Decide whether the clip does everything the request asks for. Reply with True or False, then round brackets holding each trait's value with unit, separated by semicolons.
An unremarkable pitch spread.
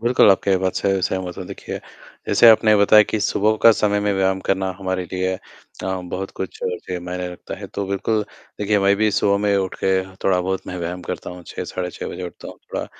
False (1.9 semitones)